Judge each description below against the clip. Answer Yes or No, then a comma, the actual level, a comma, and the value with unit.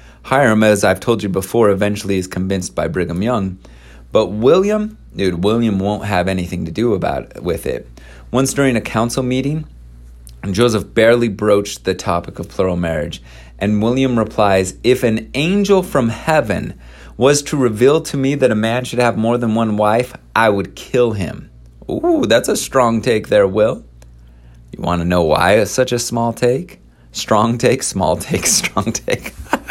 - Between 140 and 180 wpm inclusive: Yes, average, 175 wpm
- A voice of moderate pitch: No, low, 110 Hz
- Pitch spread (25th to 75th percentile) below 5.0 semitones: No, wide, 5.5 semitones